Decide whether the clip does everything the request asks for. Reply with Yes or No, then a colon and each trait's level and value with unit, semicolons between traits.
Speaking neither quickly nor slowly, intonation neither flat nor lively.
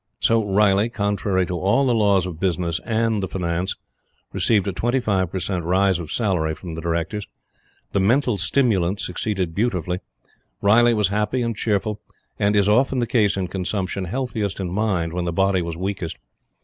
Yes: average, 175 wpm; average, 3.1 semitones